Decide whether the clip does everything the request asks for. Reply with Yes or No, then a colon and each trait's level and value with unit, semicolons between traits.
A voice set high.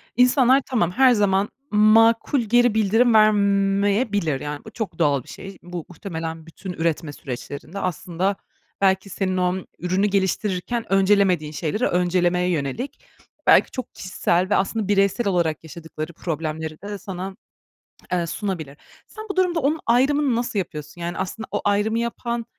Yes: high, 195 Hz